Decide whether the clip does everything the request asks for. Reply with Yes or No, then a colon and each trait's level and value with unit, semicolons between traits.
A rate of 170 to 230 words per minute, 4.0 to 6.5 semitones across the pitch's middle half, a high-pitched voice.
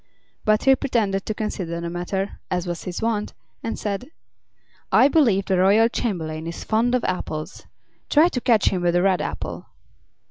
Yes: average, 175 wpm; average, 4.5 semitones; high, 195 Hz